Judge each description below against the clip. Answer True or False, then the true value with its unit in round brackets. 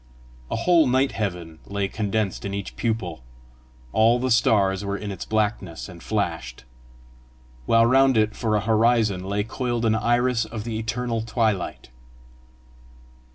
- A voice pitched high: False (110 Hz)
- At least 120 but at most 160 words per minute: True (145 wpm)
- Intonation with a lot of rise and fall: False (2.9 semitones)